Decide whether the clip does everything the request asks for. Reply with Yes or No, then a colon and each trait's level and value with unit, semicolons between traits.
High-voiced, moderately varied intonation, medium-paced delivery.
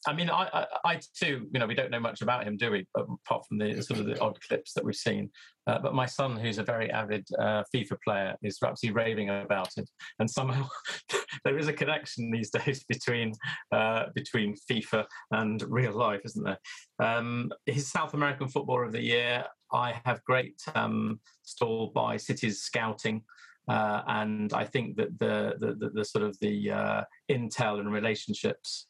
No: low, 120 Hz; average, 3.9 semitones; average, 190 wpm